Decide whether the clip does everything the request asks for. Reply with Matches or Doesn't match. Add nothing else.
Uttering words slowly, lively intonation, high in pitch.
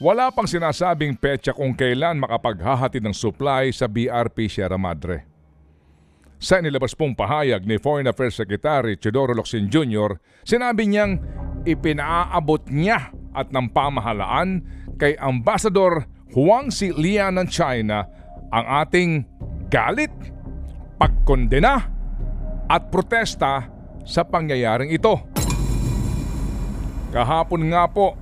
Doesn't match